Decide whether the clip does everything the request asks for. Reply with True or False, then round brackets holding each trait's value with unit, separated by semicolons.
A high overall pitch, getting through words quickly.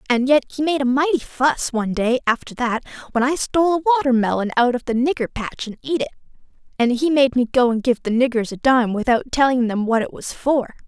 True (255 Hz; 230 wpm)